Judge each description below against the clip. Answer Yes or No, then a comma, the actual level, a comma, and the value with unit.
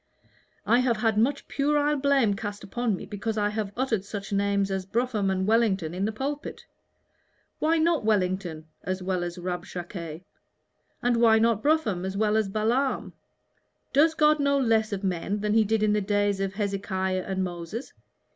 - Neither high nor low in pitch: No, high, 210 Hz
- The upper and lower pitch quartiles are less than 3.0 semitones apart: No, average, 3.7 semitones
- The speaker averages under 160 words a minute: No, average, 175 wpm